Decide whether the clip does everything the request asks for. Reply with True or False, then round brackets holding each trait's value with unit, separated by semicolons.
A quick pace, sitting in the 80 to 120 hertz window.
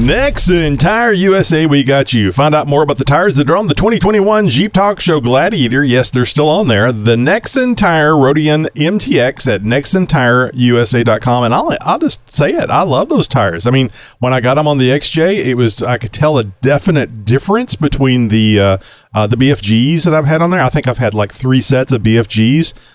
False (210 wpm; 135 Hz)